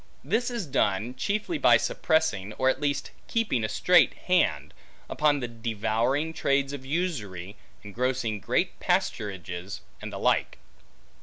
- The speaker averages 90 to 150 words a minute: Yes, slow, 135 wpm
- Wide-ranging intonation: Yes, wide, 7.0 semitones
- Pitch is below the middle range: Yes, low, 130 Hz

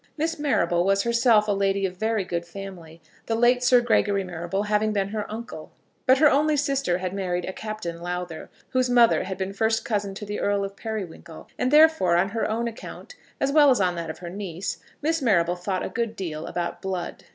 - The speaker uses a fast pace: Yes, fast, 210 wpm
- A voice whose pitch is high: Yes, high, 200 Hz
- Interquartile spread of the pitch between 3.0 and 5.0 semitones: Yes, average, 4.7 semitones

